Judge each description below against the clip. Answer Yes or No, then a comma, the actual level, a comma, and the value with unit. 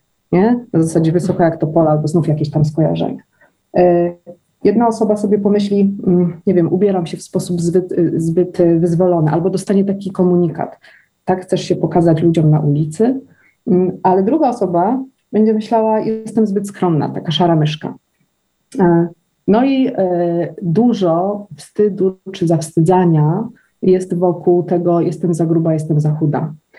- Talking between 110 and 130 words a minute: No, average, 140 wpm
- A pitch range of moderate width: Yes, average, 3.0 semitones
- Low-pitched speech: No, medium, 180 Hz